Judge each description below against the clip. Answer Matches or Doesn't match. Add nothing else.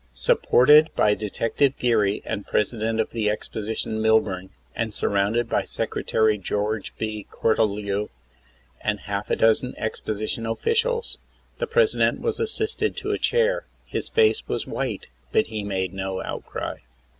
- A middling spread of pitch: Matches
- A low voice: Matches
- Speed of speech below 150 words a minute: Matches